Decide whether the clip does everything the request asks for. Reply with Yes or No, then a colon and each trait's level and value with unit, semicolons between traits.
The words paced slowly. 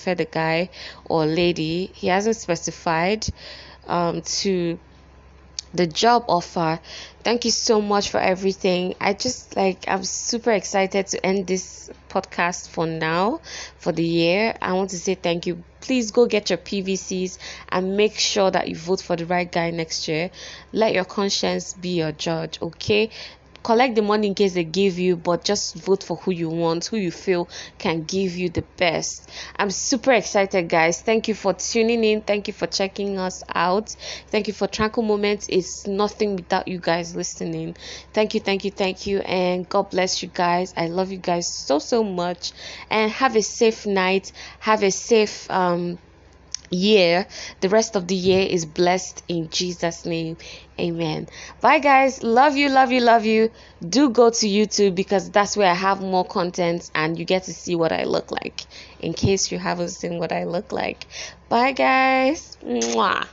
No: average, 180 wpm